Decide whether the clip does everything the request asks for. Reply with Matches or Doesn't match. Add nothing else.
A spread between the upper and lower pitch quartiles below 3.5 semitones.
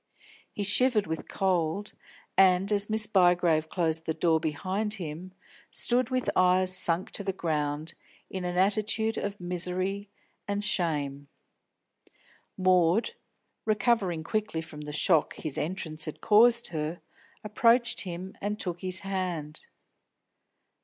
Doesn't match